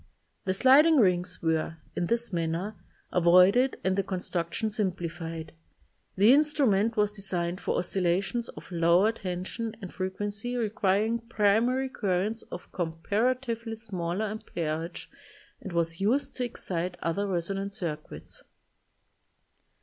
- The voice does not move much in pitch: No, average, 4.4 semitones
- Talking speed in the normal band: No, slow, 120 wpm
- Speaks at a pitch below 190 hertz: No, high, 195 Hz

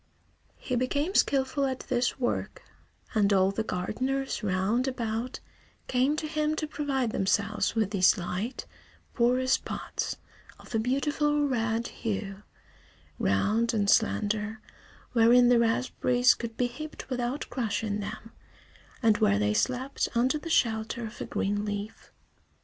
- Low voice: No, high, 235 Hz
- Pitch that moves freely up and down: No, average, 3.7 semitones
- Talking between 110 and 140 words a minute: Yes, slow, 135 wpm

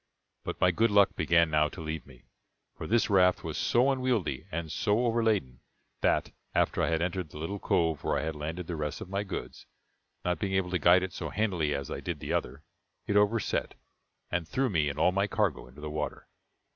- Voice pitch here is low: Yes, very low, 90 Hz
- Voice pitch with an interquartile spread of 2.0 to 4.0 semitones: No, average, 4.8 semitones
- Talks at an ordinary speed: No, fast, 215 wpm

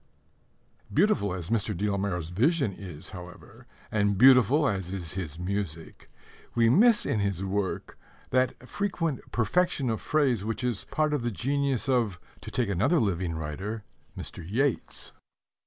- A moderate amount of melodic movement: No, wide, 6.0 semitones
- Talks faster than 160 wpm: No, average, 150 wpm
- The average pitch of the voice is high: No, low, 105 Hz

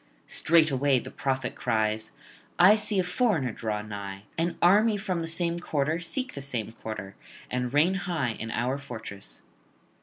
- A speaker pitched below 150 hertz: Yes, medium, 140 Hz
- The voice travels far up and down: Yes, wide, 7.6 semitones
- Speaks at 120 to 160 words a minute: Yes, average, 155 wpm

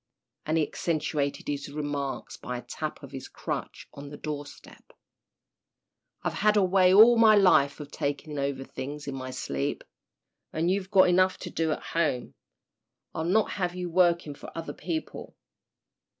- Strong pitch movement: No, average, 4.6 semitones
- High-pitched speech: No, medium, 155 Hz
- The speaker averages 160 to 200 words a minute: Yes, average, 165 wpm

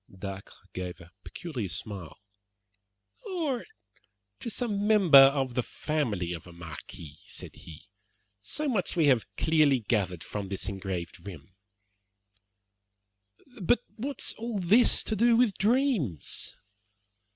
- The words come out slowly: Yes, slow, 125 wpm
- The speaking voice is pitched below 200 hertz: Yes, low, 135 Hz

